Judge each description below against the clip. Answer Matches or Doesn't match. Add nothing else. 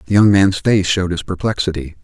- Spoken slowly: Doesn't match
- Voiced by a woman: Doesn't match